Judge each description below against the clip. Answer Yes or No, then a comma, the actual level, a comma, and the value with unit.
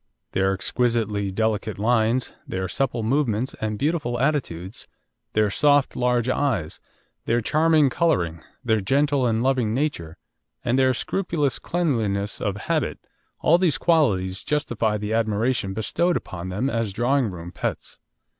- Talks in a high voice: No, low, 115 Hz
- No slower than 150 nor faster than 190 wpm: No, slow, 135 wpm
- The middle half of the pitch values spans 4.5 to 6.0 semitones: Yes, average, 5.2 semitones